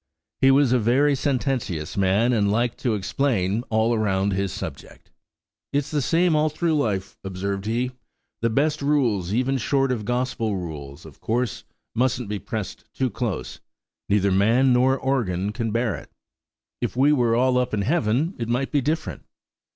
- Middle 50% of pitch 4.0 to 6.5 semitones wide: Yes, average, 4.9 semitones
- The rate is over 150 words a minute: Yes, average, 165 wpm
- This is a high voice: No, low, 120 Hz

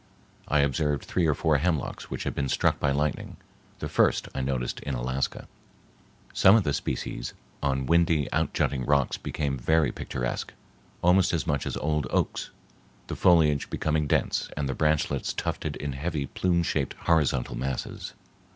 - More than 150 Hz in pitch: No, very low, 75 Hz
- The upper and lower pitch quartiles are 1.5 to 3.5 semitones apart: Yes, average, 3.0 semitones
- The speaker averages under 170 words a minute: Yes, average, 160 wpm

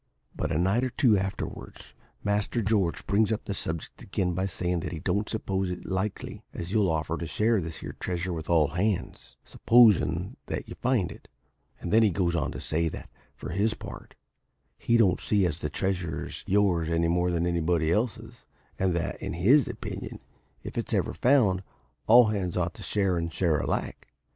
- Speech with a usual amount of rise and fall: Yes, average, 3.7 semitones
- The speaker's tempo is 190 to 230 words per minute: Yes, average, 195 wpm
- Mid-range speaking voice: No, very low, 95 Hz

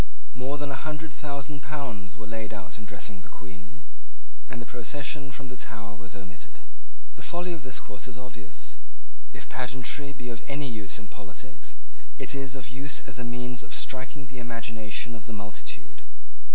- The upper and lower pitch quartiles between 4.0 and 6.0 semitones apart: Yes, average, 4.8 semitones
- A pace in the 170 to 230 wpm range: Yes, average, 180 wpm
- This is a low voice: Yes, low, 125 Hz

